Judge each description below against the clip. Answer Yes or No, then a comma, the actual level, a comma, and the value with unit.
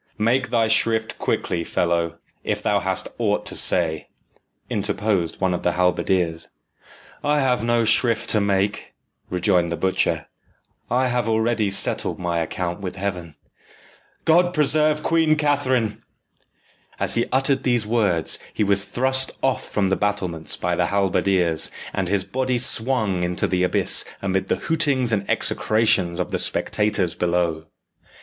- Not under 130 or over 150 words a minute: Yes, average, 145 wpm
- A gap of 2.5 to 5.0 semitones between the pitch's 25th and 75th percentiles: No, wide, 5.4 semitones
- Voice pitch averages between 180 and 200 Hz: No, low, 100 Hz